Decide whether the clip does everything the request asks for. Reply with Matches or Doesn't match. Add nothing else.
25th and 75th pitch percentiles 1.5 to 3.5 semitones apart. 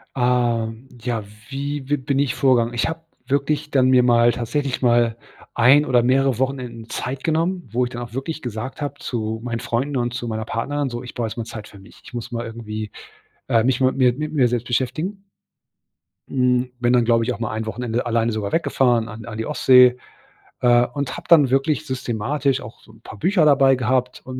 Matches